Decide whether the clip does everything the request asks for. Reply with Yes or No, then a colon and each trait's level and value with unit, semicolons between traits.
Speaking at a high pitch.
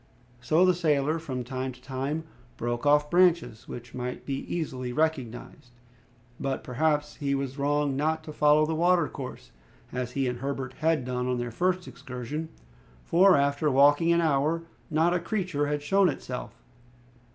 No: medium, 145 Hz